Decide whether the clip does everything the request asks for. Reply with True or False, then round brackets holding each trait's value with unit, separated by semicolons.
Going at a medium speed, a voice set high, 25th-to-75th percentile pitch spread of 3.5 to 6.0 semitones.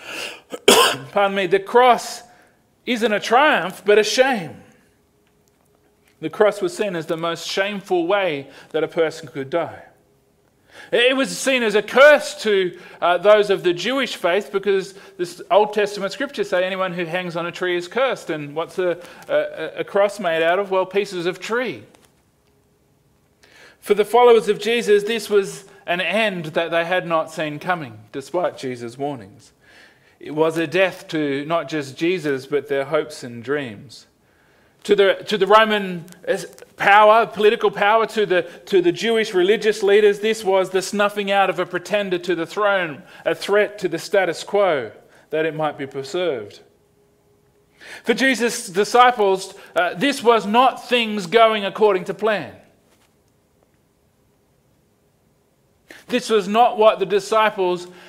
True (155 wpm; 195 Hz; 4.3 semitones)